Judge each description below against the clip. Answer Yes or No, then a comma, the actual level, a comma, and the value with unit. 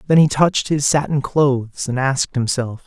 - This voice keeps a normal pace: Yes, average, 190 wpm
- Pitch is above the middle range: No, low, 135 Hz